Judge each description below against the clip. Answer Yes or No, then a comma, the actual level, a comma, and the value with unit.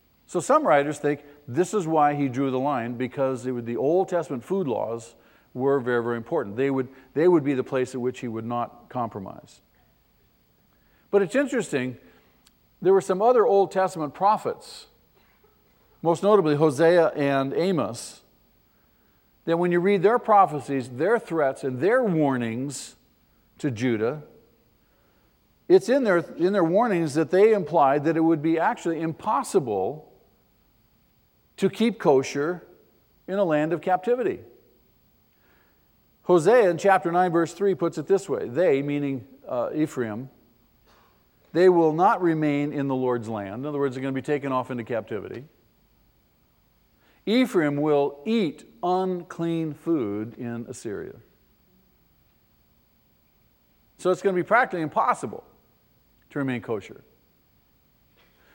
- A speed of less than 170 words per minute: Yes, average, 140 wpm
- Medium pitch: Yes, medium, 150 Hz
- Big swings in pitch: Yes, wide, 6.0 semitones